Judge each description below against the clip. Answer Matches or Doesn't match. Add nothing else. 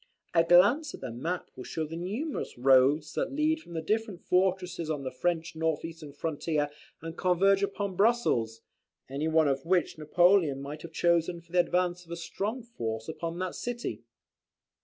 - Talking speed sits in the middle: Matches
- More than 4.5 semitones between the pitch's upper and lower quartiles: Doesn't match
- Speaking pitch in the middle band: Matches